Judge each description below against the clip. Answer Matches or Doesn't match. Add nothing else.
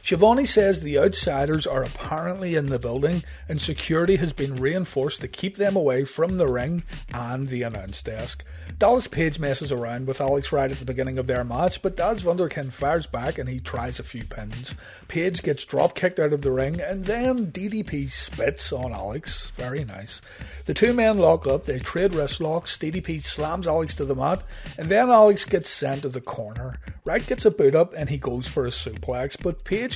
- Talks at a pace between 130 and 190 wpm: Doesn't match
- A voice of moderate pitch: Matches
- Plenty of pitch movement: Matches